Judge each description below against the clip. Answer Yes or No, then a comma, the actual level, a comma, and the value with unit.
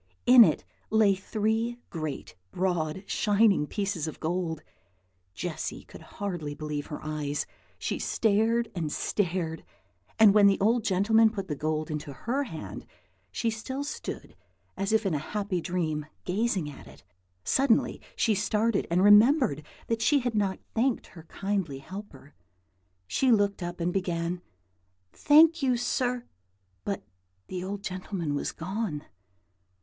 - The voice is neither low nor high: No, high, 195 Hz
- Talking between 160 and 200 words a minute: No, average, 140 wpm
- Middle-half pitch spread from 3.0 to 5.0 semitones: No, wide, 5.4 semitones